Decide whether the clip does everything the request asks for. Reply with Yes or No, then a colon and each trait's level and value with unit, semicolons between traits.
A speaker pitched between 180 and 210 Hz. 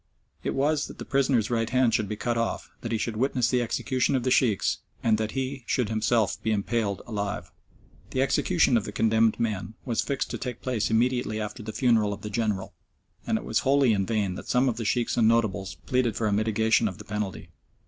No: low, 115 Hz